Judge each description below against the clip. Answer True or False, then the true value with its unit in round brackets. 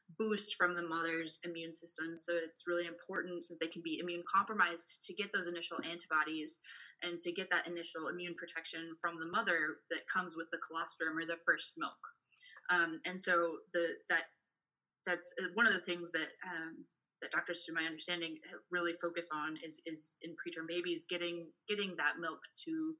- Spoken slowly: False (185 wpm)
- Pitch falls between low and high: True (170 Hz)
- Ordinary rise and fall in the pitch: False (1.3 semitones)